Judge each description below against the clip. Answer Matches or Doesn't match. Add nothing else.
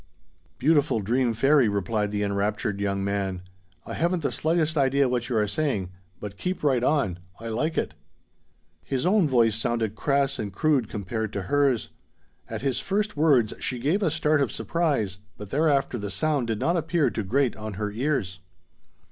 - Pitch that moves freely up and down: Matches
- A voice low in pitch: Matches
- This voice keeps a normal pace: Matches